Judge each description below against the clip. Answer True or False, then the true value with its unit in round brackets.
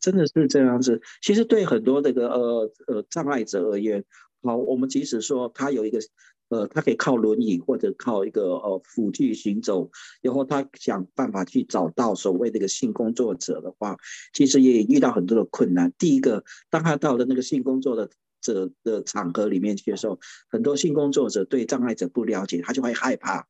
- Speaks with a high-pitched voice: False (130 Hz)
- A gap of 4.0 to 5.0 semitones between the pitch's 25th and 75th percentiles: True (4.6 semitones)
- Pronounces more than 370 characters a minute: False (300 characters per minute)